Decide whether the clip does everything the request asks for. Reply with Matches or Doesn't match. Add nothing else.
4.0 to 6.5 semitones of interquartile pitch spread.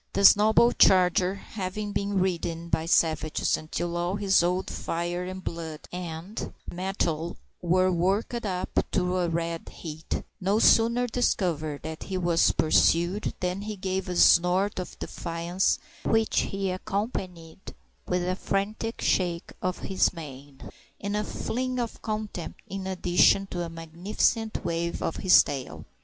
Doesn't match